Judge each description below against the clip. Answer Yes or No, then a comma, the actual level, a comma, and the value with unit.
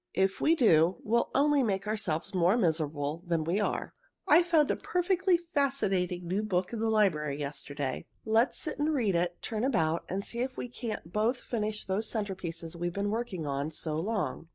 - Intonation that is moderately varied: No, wide, 6.0 semitones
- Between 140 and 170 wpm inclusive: No, average, 185 wpm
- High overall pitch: Yes, high, 200 Hz